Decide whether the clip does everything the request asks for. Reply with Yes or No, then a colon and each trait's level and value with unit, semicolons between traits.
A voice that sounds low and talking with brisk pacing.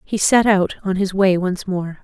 No: high, 190 Hz; fast, 235 wpm